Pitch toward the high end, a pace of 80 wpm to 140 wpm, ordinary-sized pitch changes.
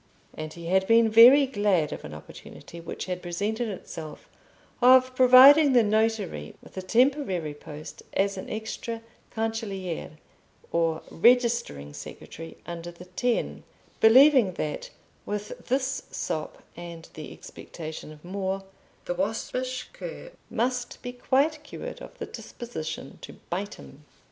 No: high, 205 Hz; slow, 135 wpm; wide, 6.6 semitones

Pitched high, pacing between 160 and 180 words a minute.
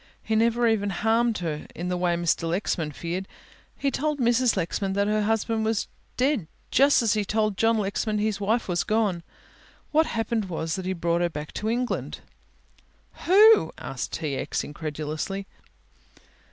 Yes: high, 210 Hz; average, 165 wpm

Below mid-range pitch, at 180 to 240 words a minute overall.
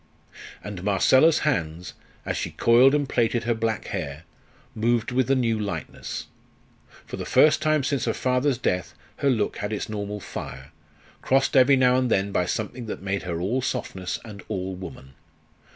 No: low, 110 Hz; average, 170 wpm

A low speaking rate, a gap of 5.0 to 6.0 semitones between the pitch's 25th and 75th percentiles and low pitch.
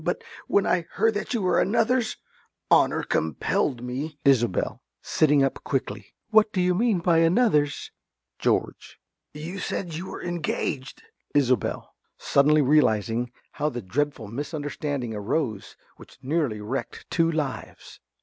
No: slow, 130 wpm; wide, 5.5 semitones; medium, 150 Hz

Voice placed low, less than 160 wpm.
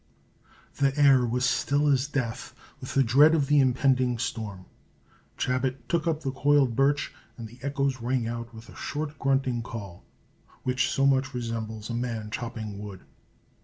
No: low, 130 Hz; average, 165 wpm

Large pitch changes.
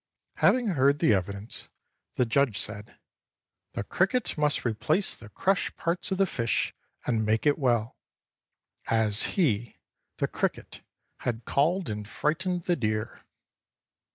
Yes: wide, 7.6 semitones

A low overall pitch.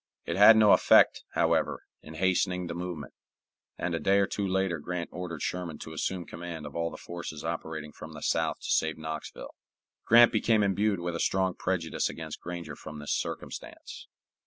Yes: very low, 85 Hz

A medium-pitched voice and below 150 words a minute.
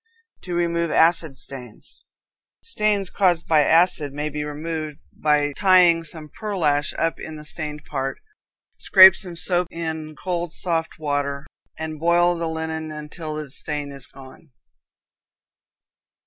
Yes: medium, 160 Hz; slow, 135 wpm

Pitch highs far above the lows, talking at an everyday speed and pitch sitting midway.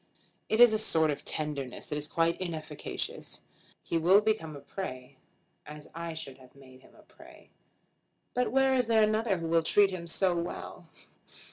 Yes: wide, 6.0 semitones; average, 175 wpm; medium, 170 Hz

